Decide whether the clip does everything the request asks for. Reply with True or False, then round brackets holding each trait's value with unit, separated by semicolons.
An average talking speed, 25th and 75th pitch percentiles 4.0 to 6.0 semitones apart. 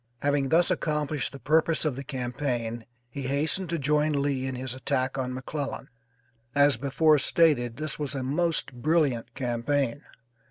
False (155 wpm; 2.9 semitones)